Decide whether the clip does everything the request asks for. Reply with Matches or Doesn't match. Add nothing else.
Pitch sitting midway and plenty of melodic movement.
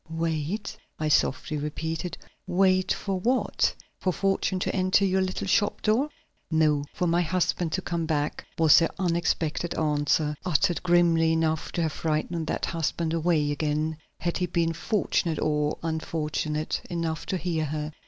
Doesn't match